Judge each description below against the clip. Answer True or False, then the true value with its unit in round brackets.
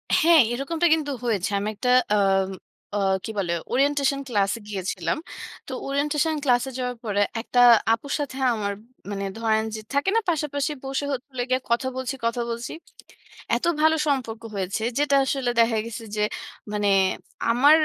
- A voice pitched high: True (250 Hz)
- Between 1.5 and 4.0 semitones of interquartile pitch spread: False (4.5 semitones)